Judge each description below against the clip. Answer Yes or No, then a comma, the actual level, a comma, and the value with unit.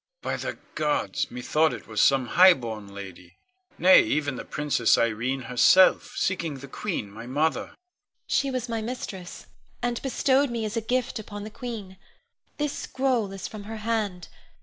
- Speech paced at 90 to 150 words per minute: No, average, 165 wpm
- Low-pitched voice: No, medium, 185 Hz